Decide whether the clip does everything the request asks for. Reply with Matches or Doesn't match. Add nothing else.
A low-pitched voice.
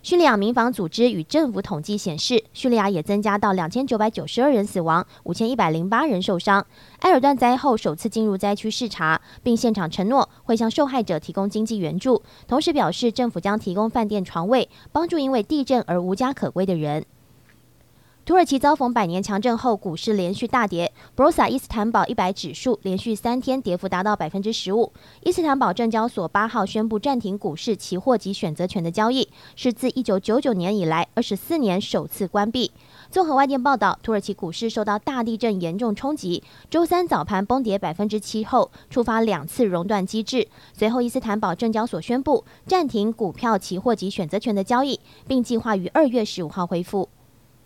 Doesn't match